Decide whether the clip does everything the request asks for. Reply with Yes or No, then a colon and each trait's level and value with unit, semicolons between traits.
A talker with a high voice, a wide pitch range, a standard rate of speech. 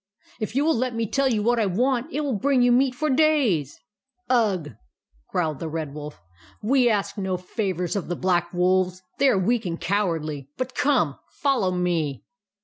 No: high, 200 Hz; wide, 6.7 semitones; fast, 210 wpm